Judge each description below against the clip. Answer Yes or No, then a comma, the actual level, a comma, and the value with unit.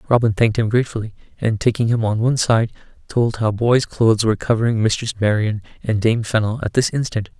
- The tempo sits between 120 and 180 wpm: No, average, 195 wpm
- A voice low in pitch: Yes, low, 115 Hz